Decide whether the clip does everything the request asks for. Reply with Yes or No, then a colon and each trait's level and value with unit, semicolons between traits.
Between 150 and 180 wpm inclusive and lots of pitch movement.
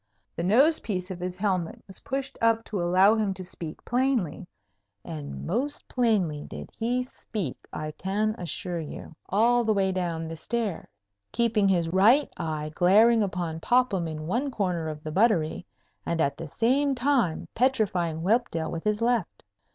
Yes: average, 160 wpm; wide, 5.8 semitones